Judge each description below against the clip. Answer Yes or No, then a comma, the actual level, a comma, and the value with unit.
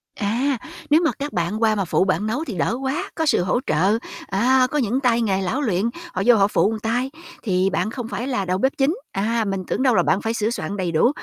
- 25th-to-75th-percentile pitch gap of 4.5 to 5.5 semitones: Yes, average, 4.9 semitones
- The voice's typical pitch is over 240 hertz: No, high, 225 Hz